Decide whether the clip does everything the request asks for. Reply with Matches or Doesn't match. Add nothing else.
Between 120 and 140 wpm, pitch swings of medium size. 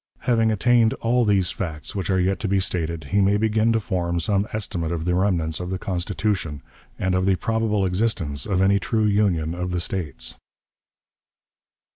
Doesn't match